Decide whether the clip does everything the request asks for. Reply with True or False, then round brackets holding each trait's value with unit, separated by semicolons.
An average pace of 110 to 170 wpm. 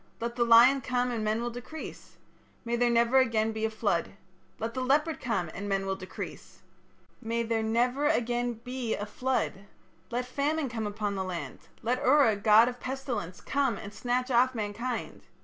False (180 wpm)